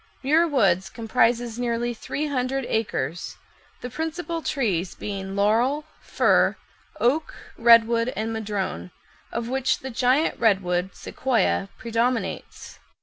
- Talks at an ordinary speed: No, slow, 110 wpm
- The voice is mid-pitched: No, high, 235 Hz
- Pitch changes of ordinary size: Yes, average, 3.9 semitones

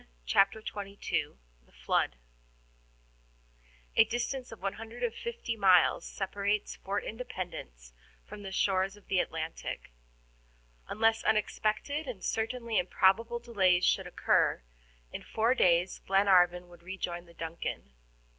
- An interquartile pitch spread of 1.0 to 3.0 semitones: No, average, 4.0 semitones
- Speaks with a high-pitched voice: Yes, high, 200 Hz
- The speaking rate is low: Yes, slow, 110 wpm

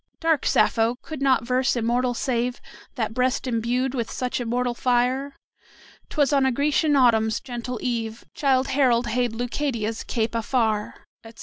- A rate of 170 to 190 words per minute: No, average, 145 wpm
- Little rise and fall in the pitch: Yes, narrow, 2.2 semitones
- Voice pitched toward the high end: Yes, high, 245 Hz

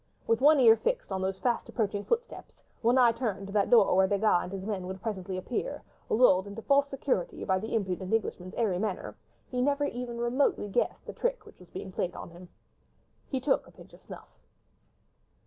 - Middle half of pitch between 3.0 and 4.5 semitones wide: No, average, 4.9 semitones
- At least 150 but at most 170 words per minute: No, average, 200 wpm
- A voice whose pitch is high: Yes, high, 220 Hz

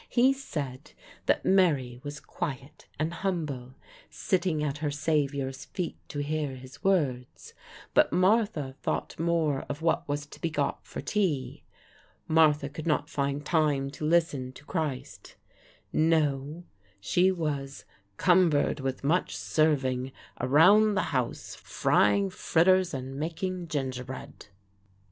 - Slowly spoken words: Yes, slow, 125 wpm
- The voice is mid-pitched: Yes, medium, 150 Hz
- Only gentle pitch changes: No, average, 3.8 semitones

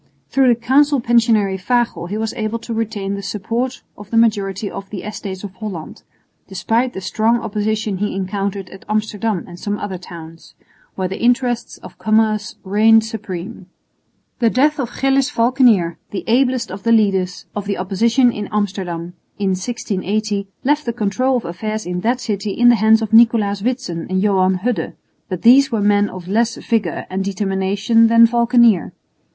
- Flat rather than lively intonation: No, average, 3.3 semitones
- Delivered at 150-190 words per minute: Yes, average, 170 wpm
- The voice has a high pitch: Yes, high, 215 Hz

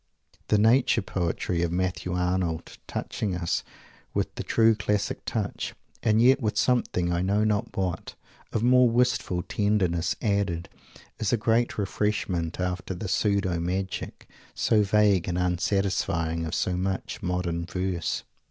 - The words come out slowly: No, average, 145 wpm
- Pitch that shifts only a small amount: No, average, 3.2 semitones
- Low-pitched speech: Yes, very low, 95 Hz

